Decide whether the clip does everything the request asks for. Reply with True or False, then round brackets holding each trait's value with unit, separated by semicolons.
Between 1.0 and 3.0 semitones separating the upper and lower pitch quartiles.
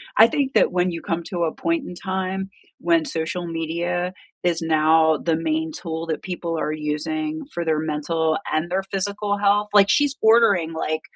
False (3.6 semitones)